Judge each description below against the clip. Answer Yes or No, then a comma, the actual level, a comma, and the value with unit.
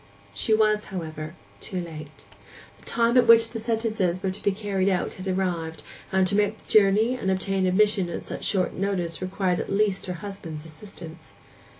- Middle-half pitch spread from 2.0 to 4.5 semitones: Yes, average, 3.1 semitones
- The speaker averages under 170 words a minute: No, average, 185 wpm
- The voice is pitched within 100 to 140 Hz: No, high, 190 Hz